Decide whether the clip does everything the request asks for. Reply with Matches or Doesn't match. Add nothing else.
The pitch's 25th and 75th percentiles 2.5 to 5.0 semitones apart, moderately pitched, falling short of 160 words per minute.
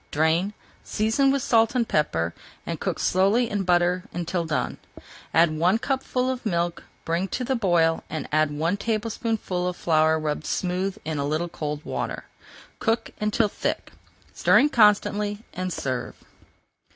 Doesn't match